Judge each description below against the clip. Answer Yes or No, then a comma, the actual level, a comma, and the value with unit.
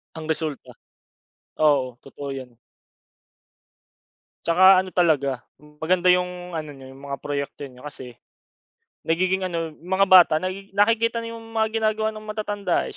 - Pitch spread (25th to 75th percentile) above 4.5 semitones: Yes, wide, 5.4 semitones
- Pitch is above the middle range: No, medium, 175 Hz